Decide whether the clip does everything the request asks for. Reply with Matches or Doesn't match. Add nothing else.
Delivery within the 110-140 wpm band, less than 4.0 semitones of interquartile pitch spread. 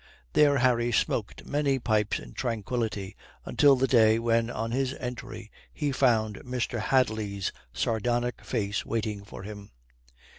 Matches